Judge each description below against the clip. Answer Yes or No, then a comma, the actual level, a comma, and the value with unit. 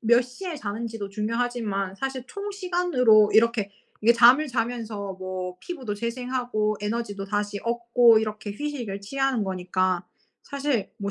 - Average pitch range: Yes, average, 3.7 semitones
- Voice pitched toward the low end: No, high, 230 Hz